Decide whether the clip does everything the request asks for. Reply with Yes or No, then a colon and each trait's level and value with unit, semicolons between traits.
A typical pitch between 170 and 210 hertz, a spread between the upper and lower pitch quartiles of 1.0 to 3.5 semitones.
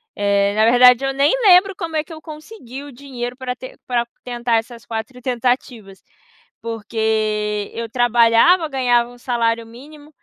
No: high, 245 Hz; average, 3.1 semitones